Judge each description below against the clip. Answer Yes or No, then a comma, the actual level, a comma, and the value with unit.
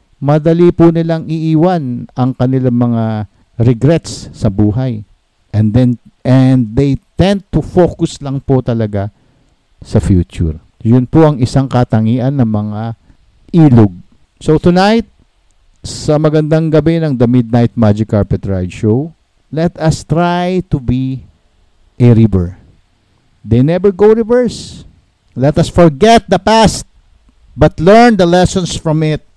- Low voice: Yes, low, 130 Hz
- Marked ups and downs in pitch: Yes, wide, 6.8 semitones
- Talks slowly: Yes, slow, 130 wpm